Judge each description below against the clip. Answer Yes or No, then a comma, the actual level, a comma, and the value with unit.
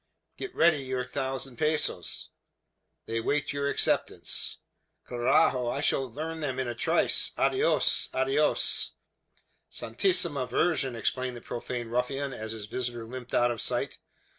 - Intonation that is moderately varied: Yes, average, 3.2 semitones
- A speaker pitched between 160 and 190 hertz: No, low, 130 Hz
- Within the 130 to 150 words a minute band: Yes, slow, 135 wpm